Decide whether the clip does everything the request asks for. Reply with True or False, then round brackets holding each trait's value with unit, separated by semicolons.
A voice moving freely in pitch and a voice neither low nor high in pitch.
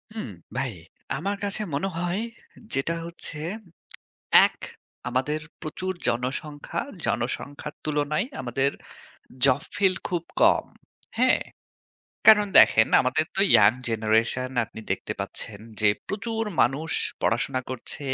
True (6.5 semitones; 145 Hz)